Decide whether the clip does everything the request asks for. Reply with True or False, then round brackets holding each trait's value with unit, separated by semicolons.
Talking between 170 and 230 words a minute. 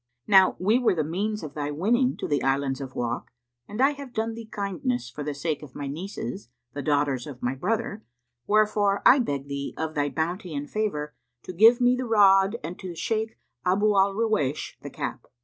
True (200 wpm)